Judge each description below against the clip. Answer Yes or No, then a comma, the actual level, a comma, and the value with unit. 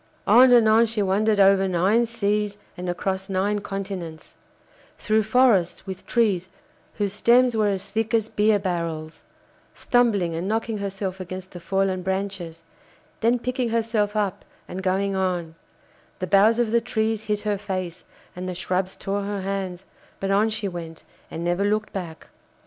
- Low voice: No, high, 200 Hz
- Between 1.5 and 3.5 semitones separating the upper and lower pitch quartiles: Yes, average, 2.8 semitones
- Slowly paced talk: No, average, 160 wpm